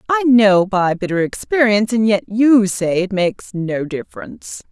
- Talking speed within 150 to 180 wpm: Yes, average, 165 wpm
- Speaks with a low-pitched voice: No, high, 210 Hz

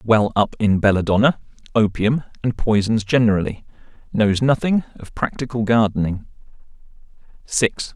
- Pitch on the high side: No, low, 110 Hz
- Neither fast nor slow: No, slow, 105 wpm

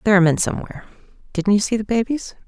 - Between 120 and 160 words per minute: No, fast, 220 wpm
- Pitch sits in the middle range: No, high, 210 Hz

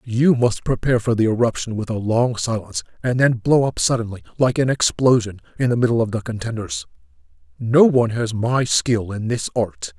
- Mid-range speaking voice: No, low, 115 Hz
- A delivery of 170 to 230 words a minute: Yes, average, 190 wpm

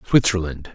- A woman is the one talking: No, male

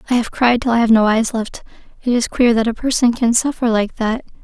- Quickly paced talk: Yes, fast, 255 wpm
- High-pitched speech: Yes, high, 235 Hz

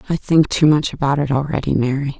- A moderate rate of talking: No, fast, 220 wpm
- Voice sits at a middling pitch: Yes, medium, 145 Hz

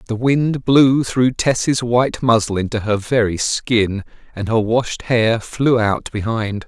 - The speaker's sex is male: Yes, male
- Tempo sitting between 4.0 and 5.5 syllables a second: No, 3.6 syllables/s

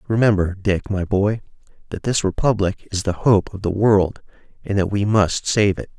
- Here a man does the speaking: Yes, male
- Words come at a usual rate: Yes, average, 190 wpm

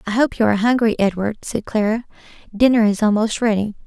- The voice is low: No, high, 220 Hz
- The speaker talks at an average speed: Yes, average, 185 wpm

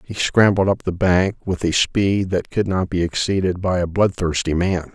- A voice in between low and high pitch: No, very low, 90 Hz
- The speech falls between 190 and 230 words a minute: Yes, fast, 205 wpm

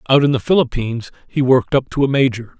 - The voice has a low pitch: Yes, low, 130 Hz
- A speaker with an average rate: No, fast, 230 wpm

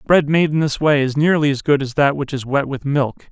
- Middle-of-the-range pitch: Yes, medium, 145 Hz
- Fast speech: Yes, fast, 290 wpm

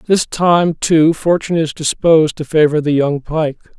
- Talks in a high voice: No, medium, 155 Hz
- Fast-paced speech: No, average, 175 wpm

